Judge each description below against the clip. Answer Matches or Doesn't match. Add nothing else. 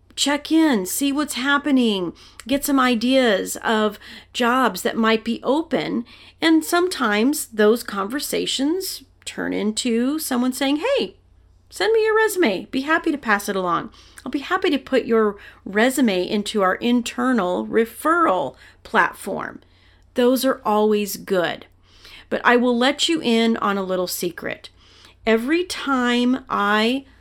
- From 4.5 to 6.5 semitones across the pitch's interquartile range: Matches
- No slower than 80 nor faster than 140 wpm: Matches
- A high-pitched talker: Matches